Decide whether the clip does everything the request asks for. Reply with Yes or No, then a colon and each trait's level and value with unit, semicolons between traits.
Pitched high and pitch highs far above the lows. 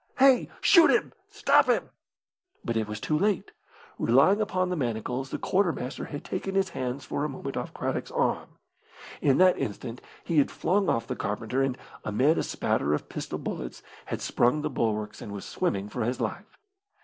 No: low, 135 Hz; wide, 8.5 semitones